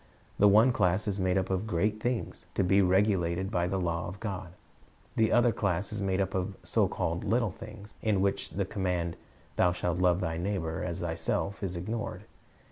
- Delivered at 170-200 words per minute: Yes, average, 195 wpm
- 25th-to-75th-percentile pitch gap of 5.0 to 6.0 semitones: No, narrow, 2.6 semitones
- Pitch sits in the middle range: No, very low, 95 Hz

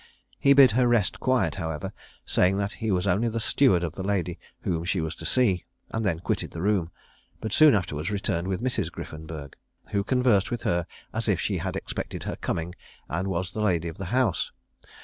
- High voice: No, very low, 95 Hz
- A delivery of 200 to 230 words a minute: Yes, fast, 205 wpm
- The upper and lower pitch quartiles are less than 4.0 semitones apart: No, average, 4.8 semitones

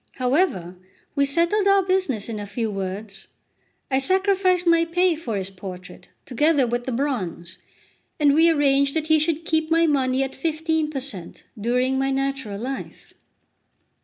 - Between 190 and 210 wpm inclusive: No, average, 160 wpm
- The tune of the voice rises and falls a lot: Yes, wide, 6.2 semitones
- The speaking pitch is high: Yes, very high, 275 Hz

